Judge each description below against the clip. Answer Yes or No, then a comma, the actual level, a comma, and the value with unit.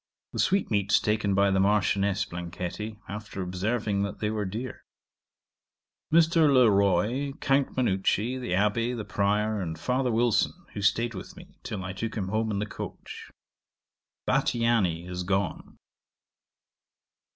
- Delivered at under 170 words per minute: Yes, average, 140 wpm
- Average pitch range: Yes, average, 3.3 semitones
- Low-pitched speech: Yes, low, 105 Hz